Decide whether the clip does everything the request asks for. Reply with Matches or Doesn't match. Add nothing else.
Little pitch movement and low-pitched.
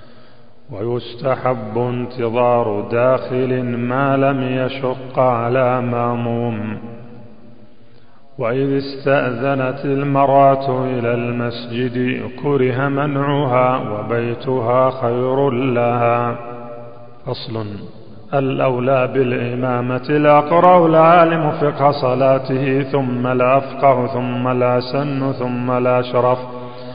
Matches